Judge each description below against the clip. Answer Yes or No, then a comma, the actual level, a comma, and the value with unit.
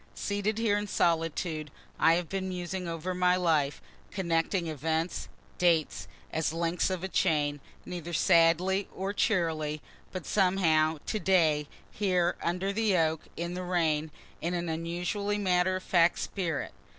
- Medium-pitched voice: Yes, medium, 175 Hz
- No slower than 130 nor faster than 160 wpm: Yes, average, 145 wpm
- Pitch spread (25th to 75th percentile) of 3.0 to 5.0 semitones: No, narrow, 2.5 semitones